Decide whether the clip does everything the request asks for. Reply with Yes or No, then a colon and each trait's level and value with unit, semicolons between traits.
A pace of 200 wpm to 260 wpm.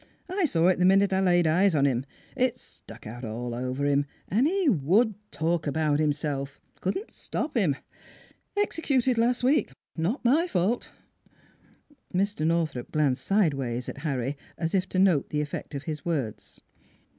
No: average, 165 wpm